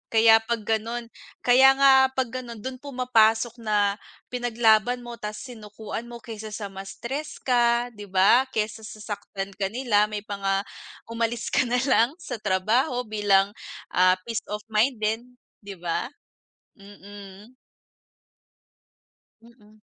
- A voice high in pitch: Yes, high, 225 Hz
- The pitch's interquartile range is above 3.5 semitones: No, average, 2.7 semitones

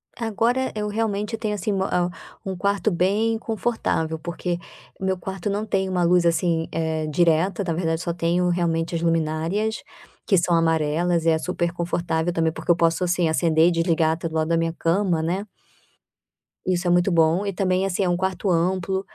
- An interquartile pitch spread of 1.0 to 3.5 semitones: Yes, average, 2.7 semitones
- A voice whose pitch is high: No, medium, 175 Hz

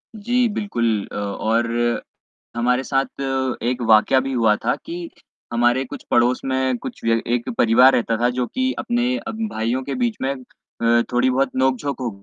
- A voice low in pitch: Yes, low, 125 Hz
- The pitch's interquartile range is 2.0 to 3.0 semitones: Yes, average, 2.7 semitones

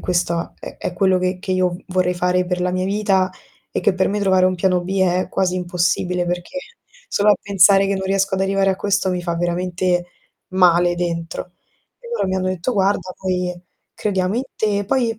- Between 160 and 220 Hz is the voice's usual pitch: Yes, medium, 185 Hz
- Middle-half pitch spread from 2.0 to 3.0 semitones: No, narrow, 1.4 semitones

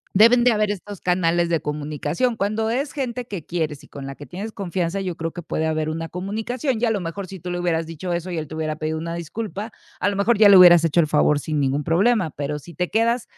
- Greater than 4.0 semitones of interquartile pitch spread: Yes, average, 4.8 semitones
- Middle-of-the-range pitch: Yes, medium, 175 Hz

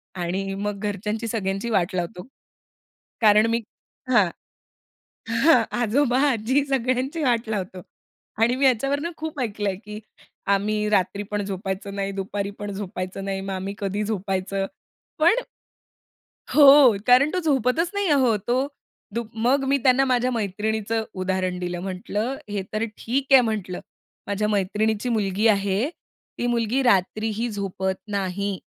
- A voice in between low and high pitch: No, high, 210 Hz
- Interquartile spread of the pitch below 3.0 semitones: No, average, 4.2 semitones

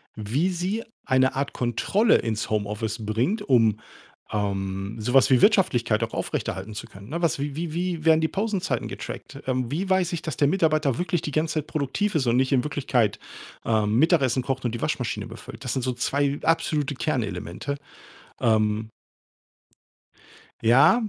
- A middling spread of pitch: No, wide, 6.2 semitones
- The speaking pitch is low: Yes, low, 130 Hz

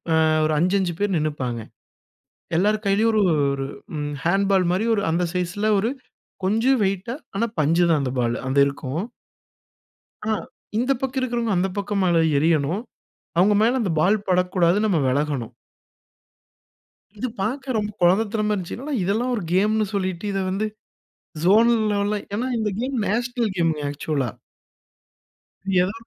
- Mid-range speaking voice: No, high, 195 Hz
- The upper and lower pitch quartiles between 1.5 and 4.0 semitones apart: No, average, 4.4 semitones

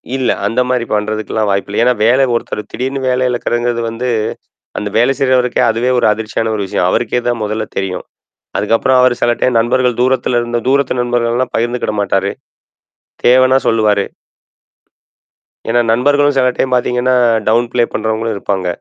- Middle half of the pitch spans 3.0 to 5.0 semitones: No, narrow, 2.5 semitones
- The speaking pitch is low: Yes, low, 120 Hz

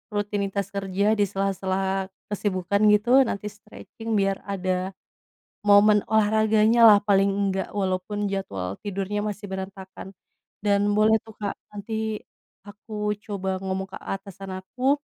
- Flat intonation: Yes, narrow, 1.6 semitones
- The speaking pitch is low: No, high, 200 Hz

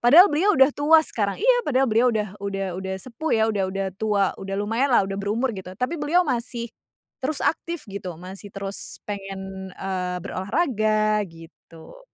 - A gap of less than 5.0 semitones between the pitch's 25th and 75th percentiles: No, wide, 5.5 semitones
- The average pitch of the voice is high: Yes, high, 215 Hz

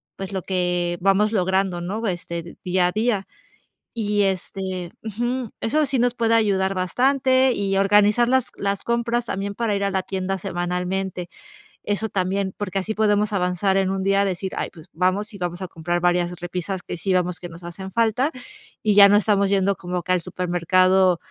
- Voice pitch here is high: Yes, high, 195 Hz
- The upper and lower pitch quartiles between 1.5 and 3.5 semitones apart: Yes, narrow, 2.6 semitones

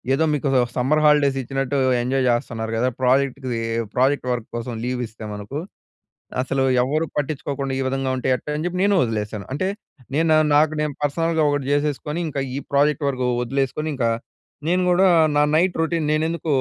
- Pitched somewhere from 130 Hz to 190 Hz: Yes, medium, 140 Hz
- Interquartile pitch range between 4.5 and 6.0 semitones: No, average, 3.2 semitones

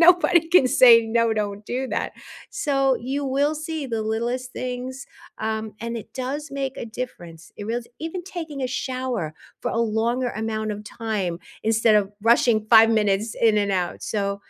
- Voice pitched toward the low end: No, high, 235 Hz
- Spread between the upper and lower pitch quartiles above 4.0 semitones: No, average, 3.6 semitones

